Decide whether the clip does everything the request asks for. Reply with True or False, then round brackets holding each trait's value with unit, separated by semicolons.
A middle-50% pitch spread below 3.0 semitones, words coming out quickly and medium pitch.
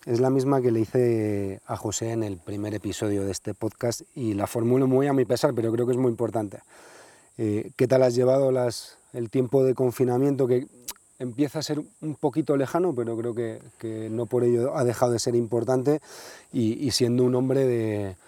False (2.6 semitones; 205 wpm; 120 Hz)